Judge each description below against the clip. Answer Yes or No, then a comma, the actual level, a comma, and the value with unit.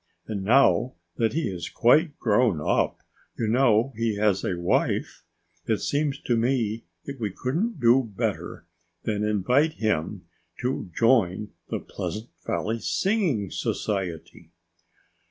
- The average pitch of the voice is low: Yes, low, 115 Hz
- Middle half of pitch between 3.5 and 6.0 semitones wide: Yes, average, 4.3 semitones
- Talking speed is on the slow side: Yes, slow, 130 wpm